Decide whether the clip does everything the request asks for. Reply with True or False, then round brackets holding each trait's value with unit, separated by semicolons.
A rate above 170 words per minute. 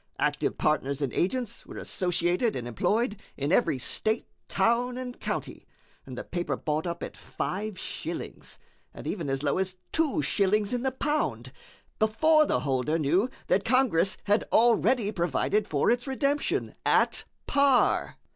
False (150 wpm)